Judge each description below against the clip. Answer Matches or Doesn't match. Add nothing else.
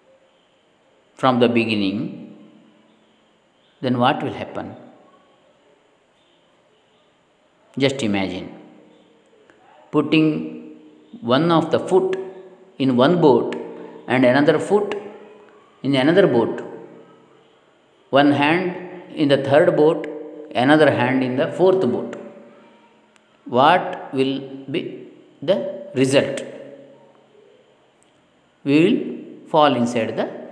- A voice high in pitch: Doesn't match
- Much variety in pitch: Matches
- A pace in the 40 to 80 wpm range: Doesn't match